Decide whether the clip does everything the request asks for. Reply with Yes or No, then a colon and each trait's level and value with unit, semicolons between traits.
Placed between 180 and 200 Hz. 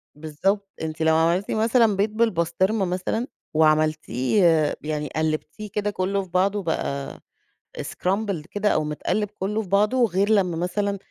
Yes: medium, 185 Hz